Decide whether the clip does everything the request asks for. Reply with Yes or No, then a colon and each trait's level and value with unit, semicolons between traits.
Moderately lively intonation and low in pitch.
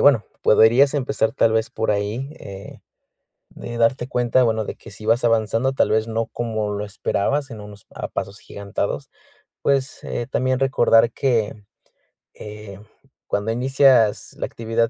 Yes: average, 3.1 semitones; low, 115 Hz